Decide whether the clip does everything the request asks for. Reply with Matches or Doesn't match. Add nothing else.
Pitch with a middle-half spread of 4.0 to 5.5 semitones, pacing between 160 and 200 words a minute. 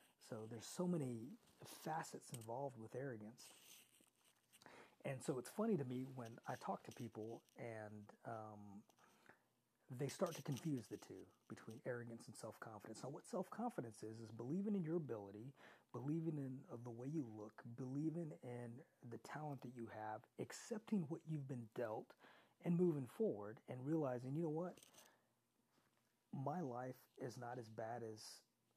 Doesn't match